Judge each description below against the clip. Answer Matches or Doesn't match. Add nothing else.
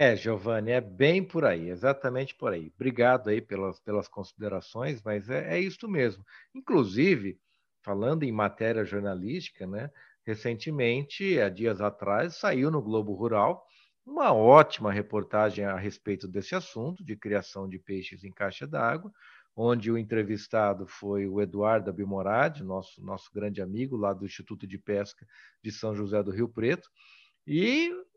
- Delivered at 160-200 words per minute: Doesn't match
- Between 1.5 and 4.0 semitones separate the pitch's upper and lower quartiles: Doesn't match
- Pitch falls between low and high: Doesn't match